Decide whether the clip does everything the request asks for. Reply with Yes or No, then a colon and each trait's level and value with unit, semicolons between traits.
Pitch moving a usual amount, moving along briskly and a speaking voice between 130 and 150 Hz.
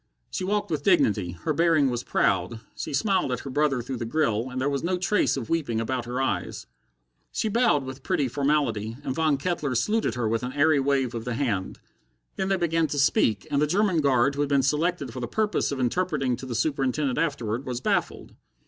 Yes: average, 4.5 semitones; fast, 215 wpm; medium, 140 Hz